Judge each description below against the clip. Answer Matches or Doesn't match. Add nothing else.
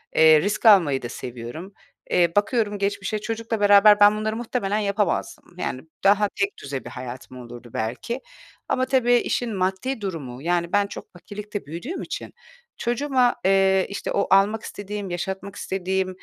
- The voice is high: Matches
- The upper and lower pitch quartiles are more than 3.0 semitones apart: Matches